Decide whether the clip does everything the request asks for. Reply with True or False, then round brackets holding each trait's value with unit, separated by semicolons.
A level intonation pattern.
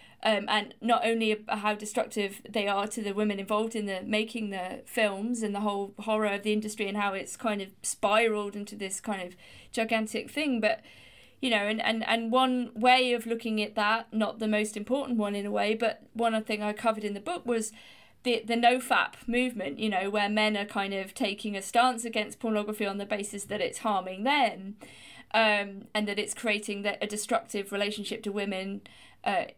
True (1.9 semitones)